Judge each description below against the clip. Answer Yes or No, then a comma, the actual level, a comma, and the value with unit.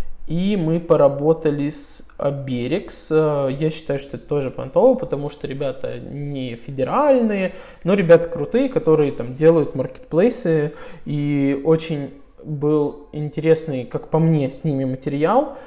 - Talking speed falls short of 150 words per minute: Yes, average, 125 wpm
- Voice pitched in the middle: Yes, medium, 150 Hz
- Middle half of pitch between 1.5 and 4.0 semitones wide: Yes, average, 2.8 semitones